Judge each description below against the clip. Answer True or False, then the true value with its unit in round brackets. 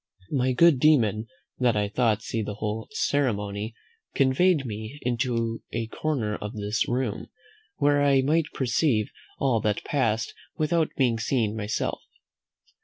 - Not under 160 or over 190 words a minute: False (135 wpm)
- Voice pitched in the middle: False (120 Hz)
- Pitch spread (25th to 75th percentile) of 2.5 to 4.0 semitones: False (4.6 semitones)